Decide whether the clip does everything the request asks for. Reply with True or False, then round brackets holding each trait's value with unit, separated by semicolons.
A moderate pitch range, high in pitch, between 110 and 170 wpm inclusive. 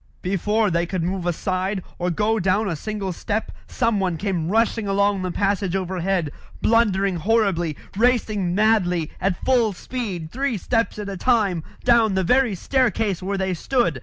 True (3.6 semitones; 195 Hz; 160 wpm)